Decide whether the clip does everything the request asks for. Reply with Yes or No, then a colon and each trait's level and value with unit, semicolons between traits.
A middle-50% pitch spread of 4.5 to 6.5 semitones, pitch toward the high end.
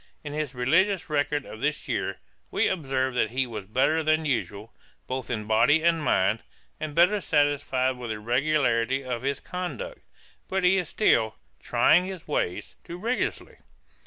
No: average, 5.1 semitones; medium, 145 Hz